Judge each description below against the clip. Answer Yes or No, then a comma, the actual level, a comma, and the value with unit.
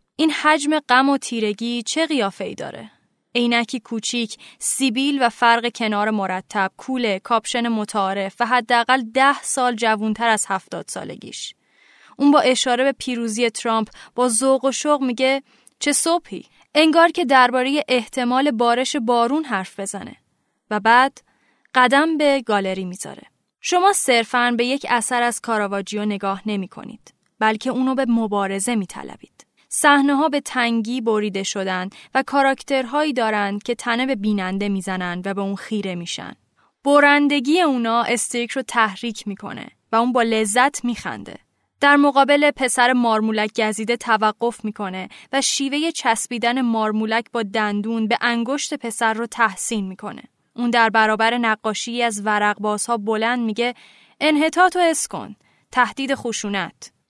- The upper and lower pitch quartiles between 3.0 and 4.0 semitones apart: Yes, average, 3.7 semitones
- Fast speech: No, average, 140 wpm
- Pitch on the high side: Yes, high, 235 Hz